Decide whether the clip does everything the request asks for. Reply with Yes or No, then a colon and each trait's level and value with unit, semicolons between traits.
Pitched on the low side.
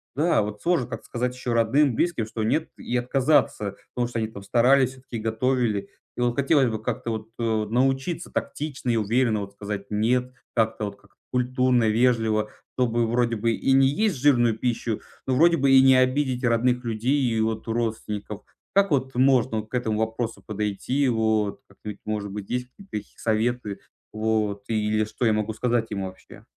Yes: low, 115 Hz